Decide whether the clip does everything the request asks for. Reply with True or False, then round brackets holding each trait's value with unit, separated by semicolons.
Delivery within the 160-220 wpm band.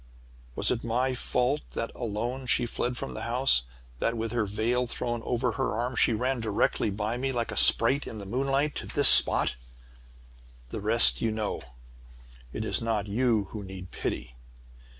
True (175 wpm)